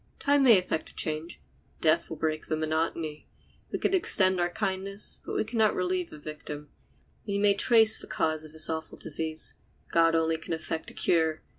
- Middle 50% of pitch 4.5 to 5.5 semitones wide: No, average, 3.9 semitones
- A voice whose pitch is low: No, medium, 165 Hz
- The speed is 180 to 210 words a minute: Yes, average, 185 wpm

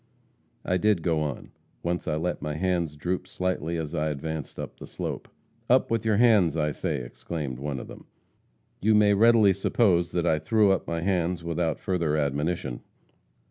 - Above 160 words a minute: Yes, average, 180 wpm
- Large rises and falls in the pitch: No, average, 3.8 semitones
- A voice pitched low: Yes, very low, 85 Hz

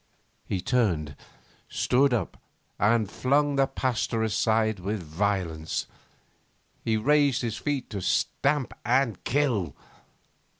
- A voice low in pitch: Yes, low, 115 Hz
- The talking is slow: Yes, slow, 110 wpm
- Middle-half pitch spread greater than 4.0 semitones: Yes, average, 5.0 semitones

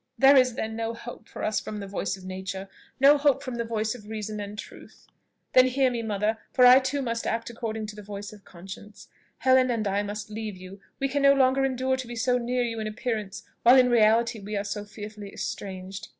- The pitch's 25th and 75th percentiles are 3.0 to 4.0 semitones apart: Yes, average, 3.4 semitones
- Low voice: No, high, 220 Hz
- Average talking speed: No, fast, 235 wpm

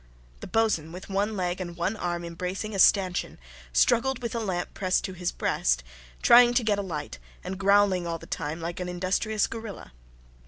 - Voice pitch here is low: No, medium, 185 Hz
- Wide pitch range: No, average, 3.5 semitones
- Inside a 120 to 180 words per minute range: No, average, 190 wpm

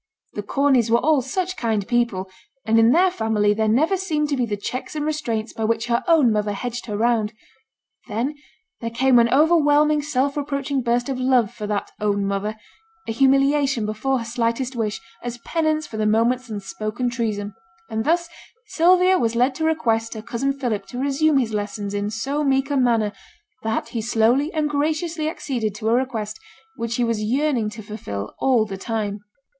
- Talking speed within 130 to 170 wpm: No, average, 185 wpm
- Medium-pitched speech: No, high, 240 Hz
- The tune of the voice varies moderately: Yes, average, 4.4 semitones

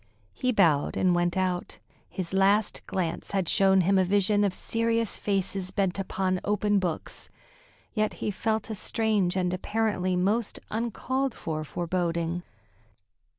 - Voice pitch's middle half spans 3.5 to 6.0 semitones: No, average, 2.9 semitones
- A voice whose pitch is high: Yes, high, 195 Hz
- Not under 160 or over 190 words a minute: No, average, 140 wpm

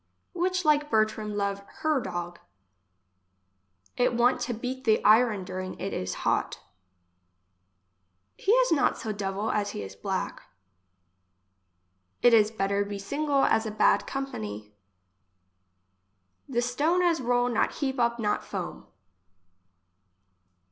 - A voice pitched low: No, high, 230 Hz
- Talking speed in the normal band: No, slow, 125 wpm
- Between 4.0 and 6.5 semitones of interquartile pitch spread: Yes, average, 5.2 semitones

